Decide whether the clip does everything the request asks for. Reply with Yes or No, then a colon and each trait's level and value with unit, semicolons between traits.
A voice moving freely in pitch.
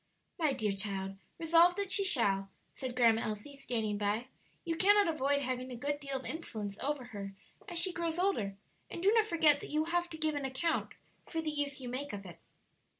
Yes: wide, 6.9 semitones